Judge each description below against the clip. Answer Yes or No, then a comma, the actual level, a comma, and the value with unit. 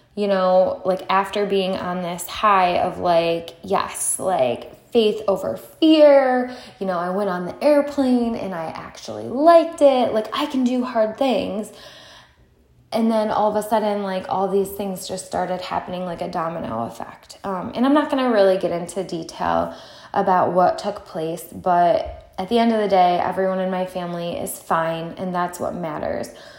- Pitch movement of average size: Yes, average, 4.7 semitones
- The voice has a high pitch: Yes, high, 195 Hz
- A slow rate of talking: No, average, 185 wpm